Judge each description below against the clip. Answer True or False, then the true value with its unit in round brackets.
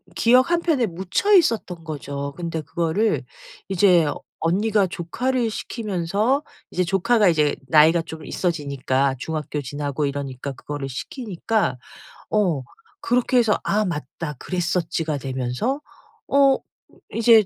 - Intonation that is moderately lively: False (7.0 semitones)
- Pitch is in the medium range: True (175 Hz)